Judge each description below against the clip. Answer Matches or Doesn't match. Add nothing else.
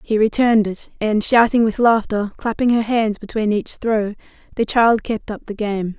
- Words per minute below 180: Doesn't match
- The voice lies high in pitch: Matches